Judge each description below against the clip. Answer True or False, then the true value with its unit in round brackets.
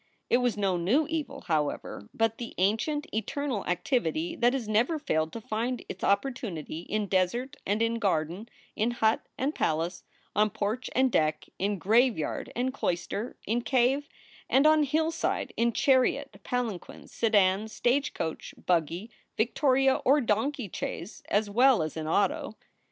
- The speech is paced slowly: False (150 wpm)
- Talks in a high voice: True (225 Hz)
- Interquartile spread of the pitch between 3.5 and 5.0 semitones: False (5.5 semitones)